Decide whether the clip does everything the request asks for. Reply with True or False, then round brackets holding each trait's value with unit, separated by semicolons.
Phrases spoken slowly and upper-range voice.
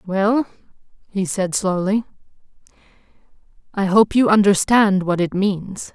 True (110 wpm; 195 Hz)